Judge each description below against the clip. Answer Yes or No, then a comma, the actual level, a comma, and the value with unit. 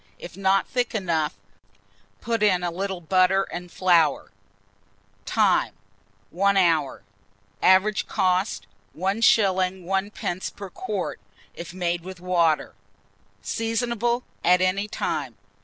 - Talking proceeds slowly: Yes, slow, 105 wpm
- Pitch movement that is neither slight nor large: No, narrow, 2.3 semitones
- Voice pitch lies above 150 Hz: Yes, medium, 185 Hz